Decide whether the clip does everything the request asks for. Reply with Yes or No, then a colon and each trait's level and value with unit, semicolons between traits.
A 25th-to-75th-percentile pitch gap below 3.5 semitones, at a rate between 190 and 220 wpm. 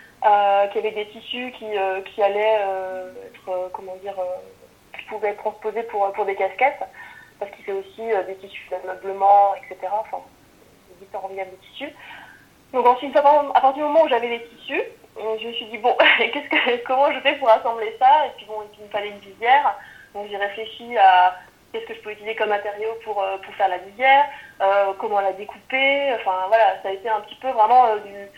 No: average, 3.9 semitones; average, 215 wpm